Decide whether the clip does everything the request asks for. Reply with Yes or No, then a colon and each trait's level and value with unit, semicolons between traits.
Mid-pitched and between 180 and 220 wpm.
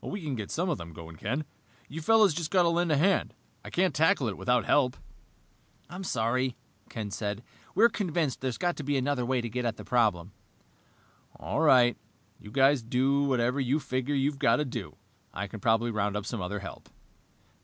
No: low, 130 Hz; average, 200 wpm